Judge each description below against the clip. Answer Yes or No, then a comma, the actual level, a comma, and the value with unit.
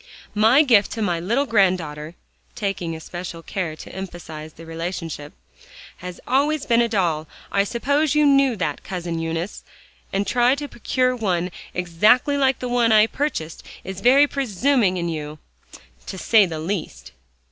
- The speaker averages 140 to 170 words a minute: Yes, average, 160 wpm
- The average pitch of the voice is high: Yes, high, 195 Hz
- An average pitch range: No, wide, 6.9 semitones